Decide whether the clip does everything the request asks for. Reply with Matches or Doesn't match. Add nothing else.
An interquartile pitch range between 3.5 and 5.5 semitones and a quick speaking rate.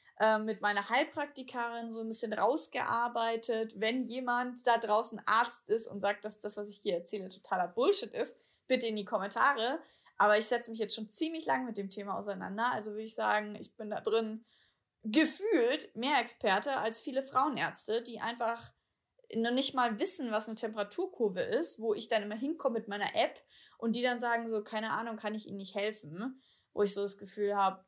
Doesn't match